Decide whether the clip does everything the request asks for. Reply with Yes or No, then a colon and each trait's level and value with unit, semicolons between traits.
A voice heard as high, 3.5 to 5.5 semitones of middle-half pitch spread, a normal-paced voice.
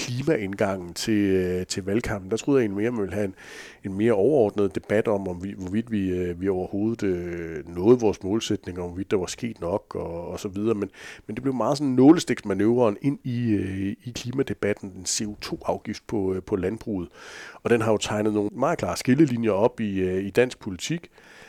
No: low, 105 Hz; average, 3.8 semitones; average, 195 wpm